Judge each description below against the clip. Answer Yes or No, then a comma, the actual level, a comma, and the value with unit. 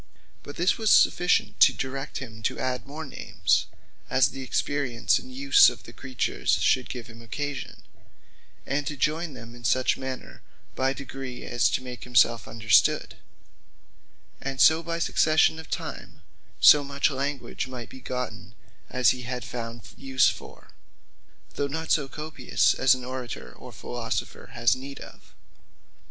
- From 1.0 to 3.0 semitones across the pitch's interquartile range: Yes, average, 2.7 semitones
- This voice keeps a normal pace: Yes, average, 155 wpm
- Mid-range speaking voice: No, low, 130 Hz